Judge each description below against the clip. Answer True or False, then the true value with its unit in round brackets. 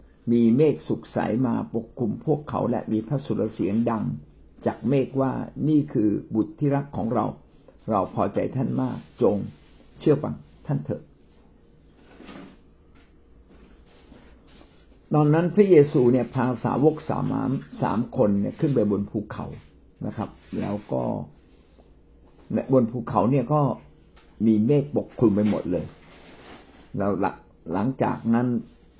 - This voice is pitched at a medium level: False (120 Hz)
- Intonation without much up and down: False (5.0 semitones)